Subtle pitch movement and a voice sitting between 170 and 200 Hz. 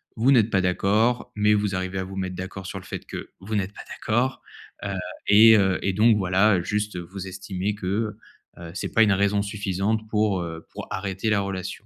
No: narrow, 2.2 semitones; low, 100 Hz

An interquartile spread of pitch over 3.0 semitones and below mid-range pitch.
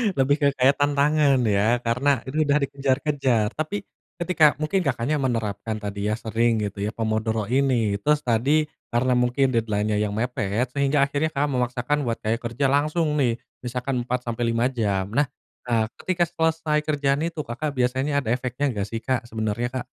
Yes: average, 4.2 semitones; low, 125 Hz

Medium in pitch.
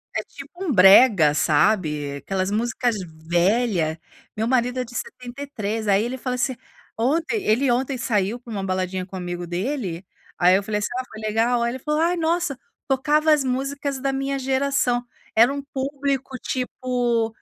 No: high, 245 Hz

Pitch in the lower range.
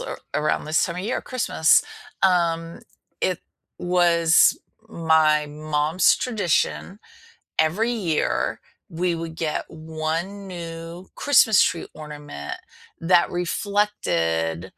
No: medium, 165 Hz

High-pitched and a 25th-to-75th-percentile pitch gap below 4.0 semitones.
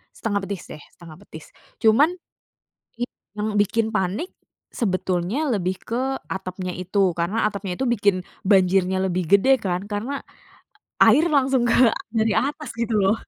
No: high, 205 Hz; average, 4.4 semitones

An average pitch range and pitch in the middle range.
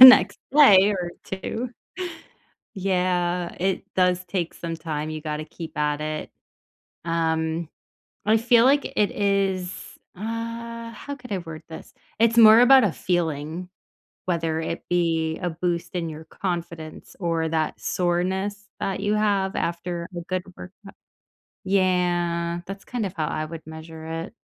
Yes: average, 3.4 semitones; medium, 180 Hz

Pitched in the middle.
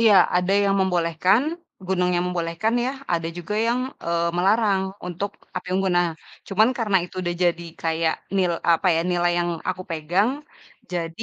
Yes: medium, 180 Hz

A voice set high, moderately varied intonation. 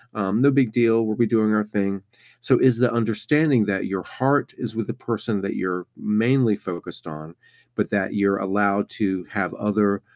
No: low, 105 Hz; average, 3.0 semitones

